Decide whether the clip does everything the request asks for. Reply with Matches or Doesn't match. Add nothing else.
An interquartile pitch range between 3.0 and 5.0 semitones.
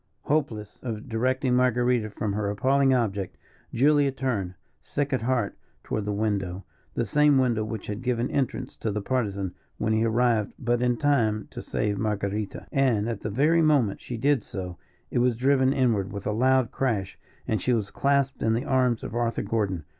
Matches